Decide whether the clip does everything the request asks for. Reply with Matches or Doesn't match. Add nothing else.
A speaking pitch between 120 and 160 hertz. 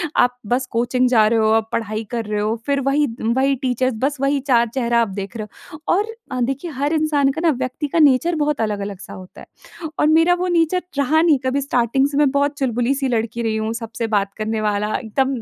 Doesn't match